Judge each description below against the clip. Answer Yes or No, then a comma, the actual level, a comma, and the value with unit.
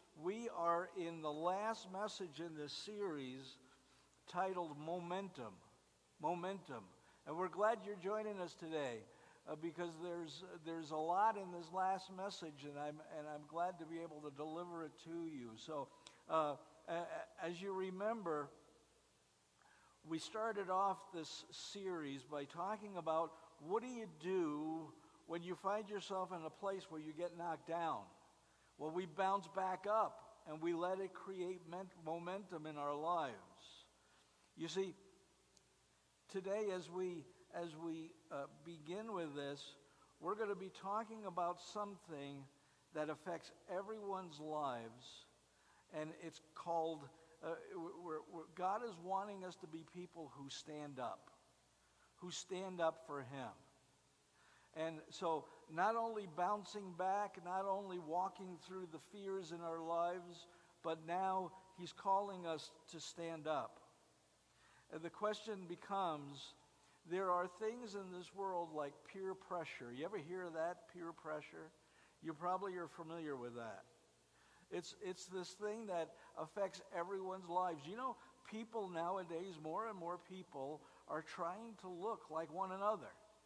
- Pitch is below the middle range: No, medium, 170 Hz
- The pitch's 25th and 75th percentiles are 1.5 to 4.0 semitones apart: Yes, average, 3.3 semitones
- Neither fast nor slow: Yes, average, 145 wpm